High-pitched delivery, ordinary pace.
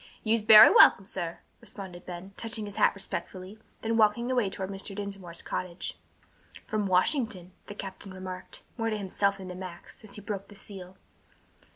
Yes: high, 195 Hz; average, 170 wpm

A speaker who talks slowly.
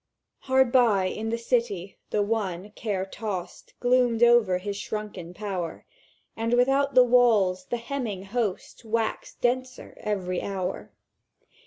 Yes: slow, 130 wpm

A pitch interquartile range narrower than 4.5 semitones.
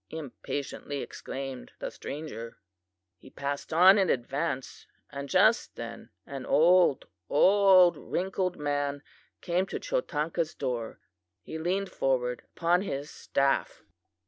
No: average, 4.9 semitones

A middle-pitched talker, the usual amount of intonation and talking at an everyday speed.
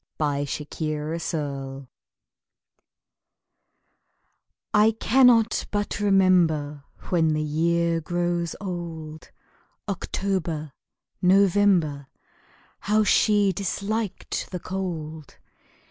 No: medium, 170 Hz; average, 4.4 semitones; slow, 80 wpm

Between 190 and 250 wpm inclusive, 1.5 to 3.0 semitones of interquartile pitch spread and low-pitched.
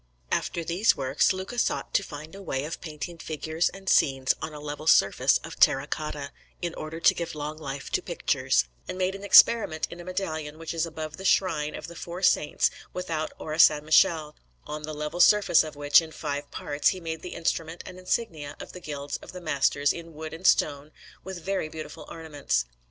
No: average, 200 wpm; average, 2.7 semitones; medium, 155 Hz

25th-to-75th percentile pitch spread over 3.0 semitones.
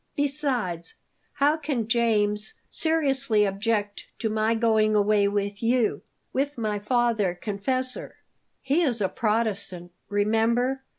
Yes: average, 3.8 semitones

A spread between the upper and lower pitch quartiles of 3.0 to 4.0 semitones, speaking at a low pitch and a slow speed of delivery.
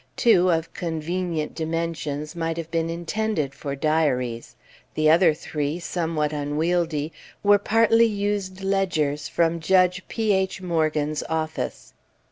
No: average, 3.3 semitones; medium, 165 Hz; slow, 120 wpm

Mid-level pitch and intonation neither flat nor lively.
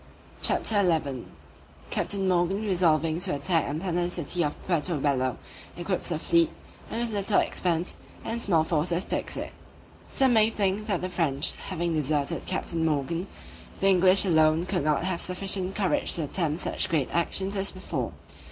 Yes: medium, 175 Hz; average, 3.4 semitones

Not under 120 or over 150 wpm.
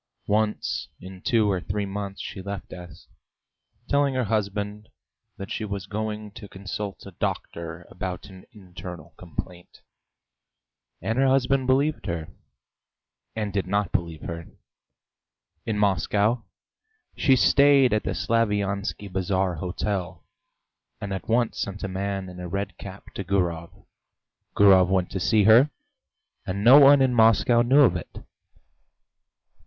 Yes: average, 140 wpm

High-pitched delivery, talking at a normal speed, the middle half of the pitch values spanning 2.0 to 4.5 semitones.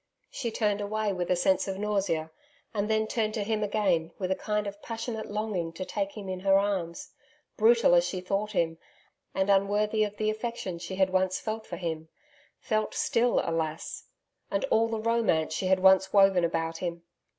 Yes: high, 195 Hz; average, 190 wpm; average, 3.1 semitones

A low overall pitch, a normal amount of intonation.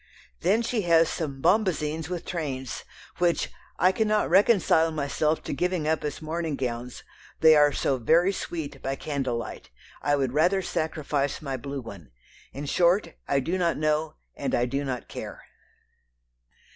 No: medium, 155 Hz; average, 3.9 semitones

